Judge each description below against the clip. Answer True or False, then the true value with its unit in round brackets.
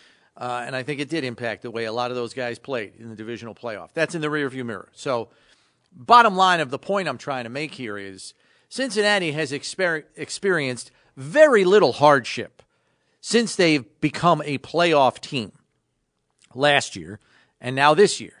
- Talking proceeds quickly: False (180 wpm)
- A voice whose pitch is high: False (140 Hz)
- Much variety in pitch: True (6.2 semitones)